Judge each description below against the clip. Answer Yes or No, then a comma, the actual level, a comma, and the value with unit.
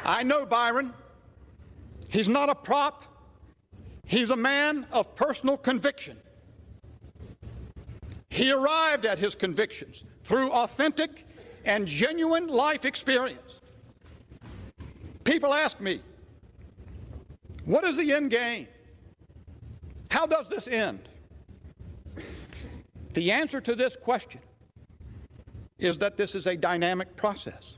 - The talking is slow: Yes, slow, 105 wpm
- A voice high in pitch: Yes, high, 235 Hz